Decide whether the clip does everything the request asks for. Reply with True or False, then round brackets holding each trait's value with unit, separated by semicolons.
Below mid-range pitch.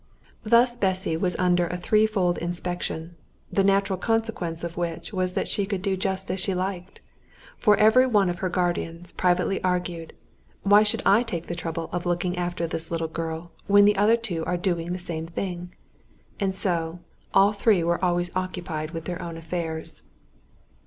False (180 Hz)